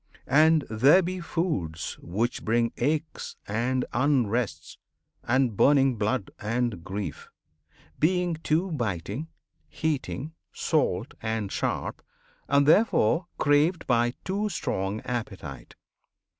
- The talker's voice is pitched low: Yes, low, 130 Hz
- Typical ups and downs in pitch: No, wide, 6.3 semitones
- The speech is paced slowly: Yes, slow, 100 wpm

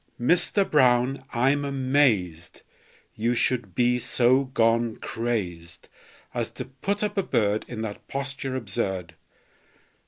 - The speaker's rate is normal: No, slow, 120 wpm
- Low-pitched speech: Yes, low, 125 Hz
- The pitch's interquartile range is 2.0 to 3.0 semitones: No, average, 3.9 semitones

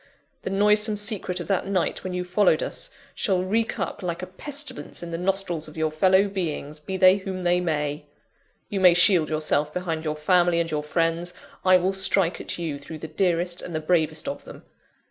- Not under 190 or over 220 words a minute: Yes, fast, 205 wpm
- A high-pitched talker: No, medium, 180 Hz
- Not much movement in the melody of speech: No, average, 3.2 semitones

